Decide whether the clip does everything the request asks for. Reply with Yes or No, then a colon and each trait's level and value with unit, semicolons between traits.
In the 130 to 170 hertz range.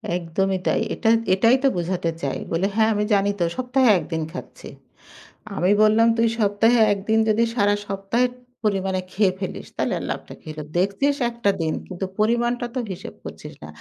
No: high, 200 Hz